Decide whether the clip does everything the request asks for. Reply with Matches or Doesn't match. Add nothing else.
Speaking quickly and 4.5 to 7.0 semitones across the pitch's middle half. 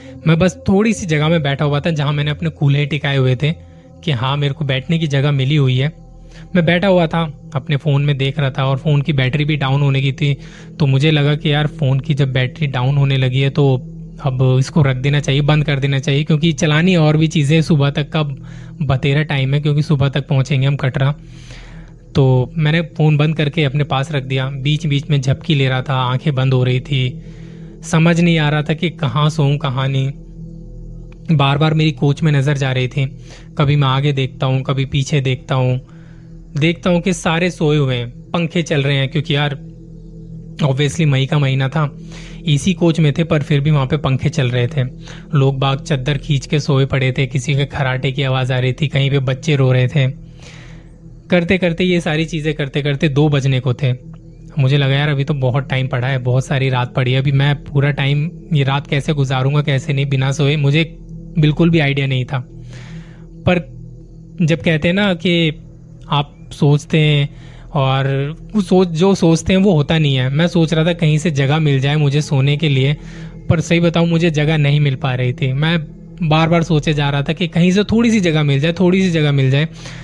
Doesn't match